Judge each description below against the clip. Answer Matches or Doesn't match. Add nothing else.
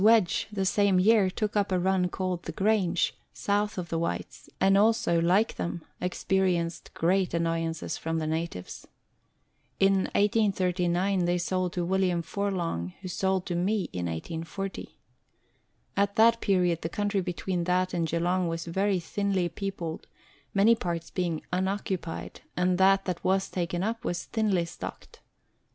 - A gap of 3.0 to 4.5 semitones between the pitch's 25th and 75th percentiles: Doesn't match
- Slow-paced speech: Doesn't match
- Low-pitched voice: Doesn't match